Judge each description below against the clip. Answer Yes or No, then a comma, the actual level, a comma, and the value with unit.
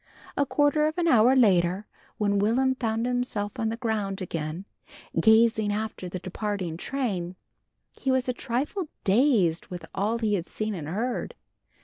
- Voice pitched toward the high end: Yes, high, 220 Hz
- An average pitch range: Yes, average, 4.6 semitones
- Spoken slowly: No, average, 155 wpm